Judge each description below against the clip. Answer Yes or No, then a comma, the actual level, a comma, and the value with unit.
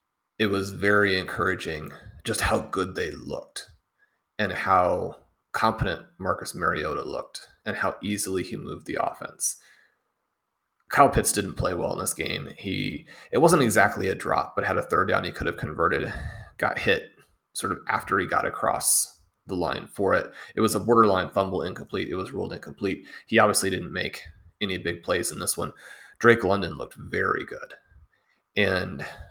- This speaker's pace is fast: No, average, 170 wpm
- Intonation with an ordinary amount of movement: No, narrow, 1.9 semitones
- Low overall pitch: Yes, low, 100 Hz